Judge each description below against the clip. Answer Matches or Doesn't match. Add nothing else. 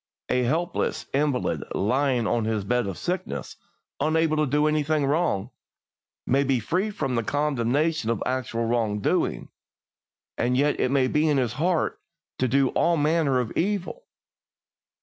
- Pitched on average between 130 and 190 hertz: Matches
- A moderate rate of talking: Matches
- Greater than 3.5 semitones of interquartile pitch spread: Matches